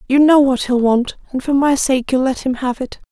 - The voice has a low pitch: No, very high, 265 Hz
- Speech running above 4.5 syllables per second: Yes, 5.2 syllables/s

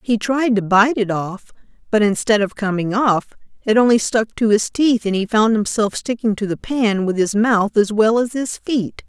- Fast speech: Yes, fast, 220 wpm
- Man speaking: No, female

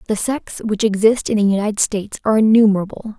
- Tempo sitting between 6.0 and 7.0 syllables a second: Yes, 6.5 syllables/s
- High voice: Yes, high, 210 Hz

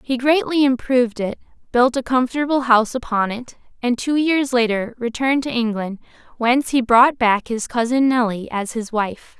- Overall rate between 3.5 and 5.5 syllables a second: Yes, 5.1 syllables/s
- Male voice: No, female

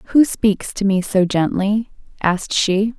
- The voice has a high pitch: Yes, high, 200 Hz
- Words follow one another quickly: No, average, 160 wpm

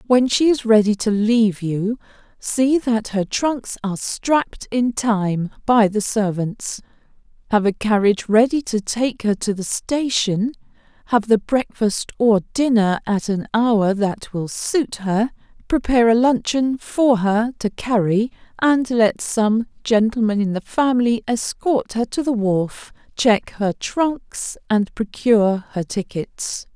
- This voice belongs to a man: No, female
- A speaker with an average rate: Yes, average, 150 wpm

